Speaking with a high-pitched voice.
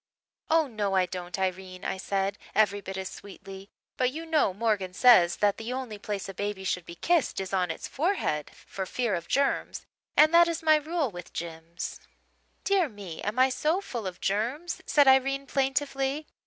Yes: high, 210 Hz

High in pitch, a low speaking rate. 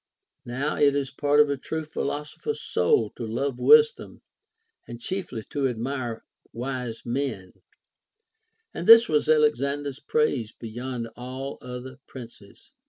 No: low, 135 Hz; slow, 125 wpm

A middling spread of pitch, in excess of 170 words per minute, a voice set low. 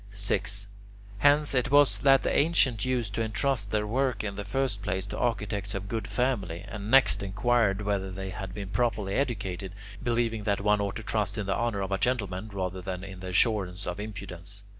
Yes: average, 3.5 semitones; average, 200 wpm; low, 105 Hz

